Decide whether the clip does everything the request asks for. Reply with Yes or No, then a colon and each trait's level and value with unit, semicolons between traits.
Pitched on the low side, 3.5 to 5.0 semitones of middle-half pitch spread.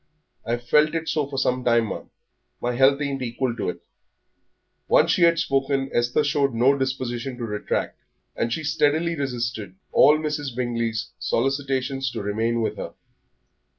No: low, 130 Hz; average, 3.1 semitones